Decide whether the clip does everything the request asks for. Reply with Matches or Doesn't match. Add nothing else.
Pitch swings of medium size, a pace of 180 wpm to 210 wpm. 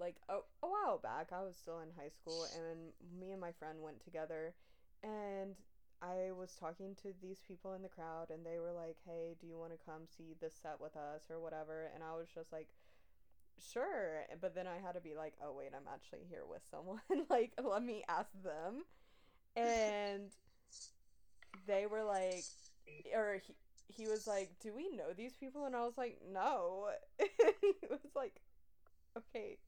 Matches